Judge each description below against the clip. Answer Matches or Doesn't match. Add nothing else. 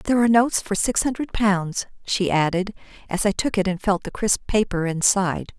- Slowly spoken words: Doesn't match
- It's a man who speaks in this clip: Doesn't match